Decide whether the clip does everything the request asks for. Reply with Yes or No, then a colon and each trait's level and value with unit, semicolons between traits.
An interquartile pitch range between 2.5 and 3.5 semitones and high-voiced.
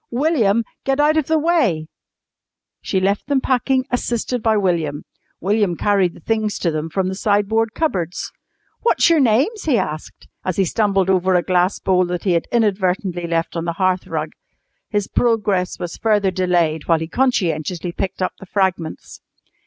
No: average, 4.5 semitones; high, 195 Hz